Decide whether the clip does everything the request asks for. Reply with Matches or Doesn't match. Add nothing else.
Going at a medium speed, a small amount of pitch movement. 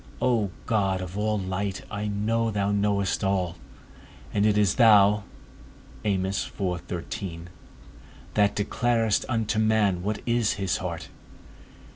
Doesn't match